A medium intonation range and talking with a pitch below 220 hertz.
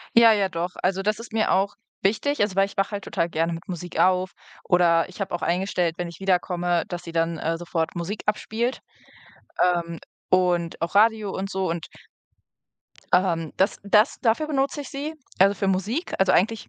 Yes: average, 3.4 semitones; high, 190 Hz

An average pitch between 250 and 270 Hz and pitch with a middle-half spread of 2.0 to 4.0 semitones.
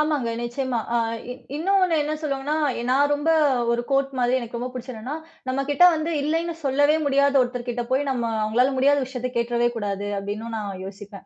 Yes: very high, 260 Hz; average, 3.3 semitones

